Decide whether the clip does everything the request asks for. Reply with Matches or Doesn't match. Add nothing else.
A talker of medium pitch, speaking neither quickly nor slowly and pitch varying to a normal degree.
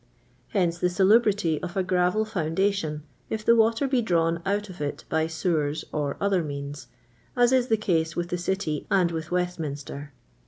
Matches